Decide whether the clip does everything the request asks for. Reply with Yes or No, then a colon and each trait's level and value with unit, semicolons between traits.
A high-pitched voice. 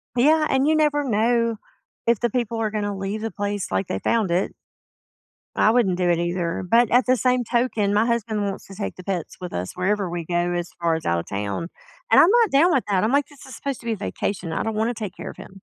Yes: high, 210 Hz